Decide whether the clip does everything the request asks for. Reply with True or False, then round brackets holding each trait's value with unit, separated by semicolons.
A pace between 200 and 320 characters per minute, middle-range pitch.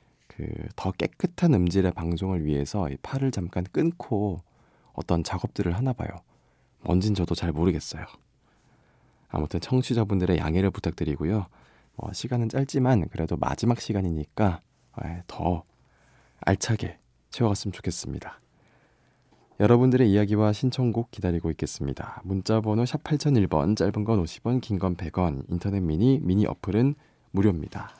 False (300 characters per minute; 95 Hz)